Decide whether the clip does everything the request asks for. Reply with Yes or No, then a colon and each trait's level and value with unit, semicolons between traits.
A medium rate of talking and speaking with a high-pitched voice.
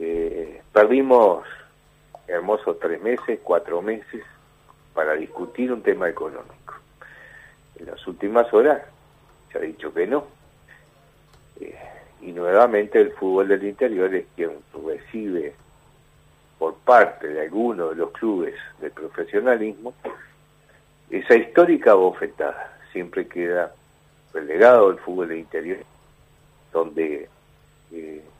No: slow, 110 wpm; very high, 385 Hz